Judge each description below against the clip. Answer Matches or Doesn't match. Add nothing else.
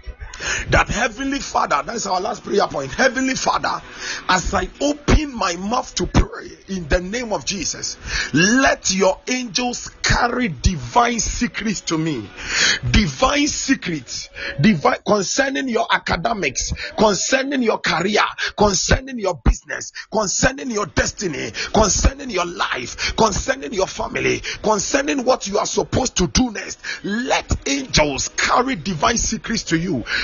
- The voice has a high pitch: Matches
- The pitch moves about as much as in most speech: Doesn't match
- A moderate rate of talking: Doesn't match